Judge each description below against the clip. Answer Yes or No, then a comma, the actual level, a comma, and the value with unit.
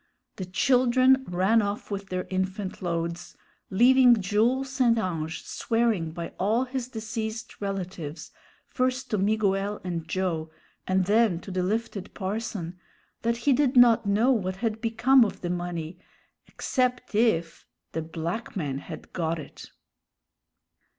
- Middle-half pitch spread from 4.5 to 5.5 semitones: Yes, average, 4.8 semitones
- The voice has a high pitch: Yes, high, 205 Hz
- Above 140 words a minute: No, slow, 135 wpm